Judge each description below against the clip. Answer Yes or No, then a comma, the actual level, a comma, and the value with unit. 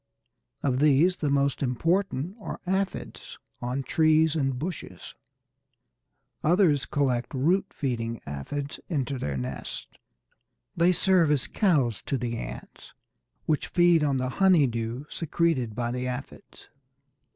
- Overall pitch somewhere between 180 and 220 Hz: No, medium, 140 Hz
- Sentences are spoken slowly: Yes, slow, 125 wpm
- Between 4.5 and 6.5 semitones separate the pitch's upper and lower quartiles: Yes, average, 5.0 semitones